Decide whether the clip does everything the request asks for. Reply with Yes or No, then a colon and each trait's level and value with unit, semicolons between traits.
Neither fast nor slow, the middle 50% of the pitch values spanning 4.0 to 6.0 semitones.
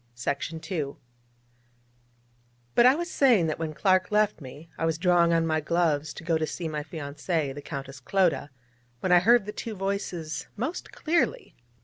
Yes: average, 160 wpm; average, 4.4 semitones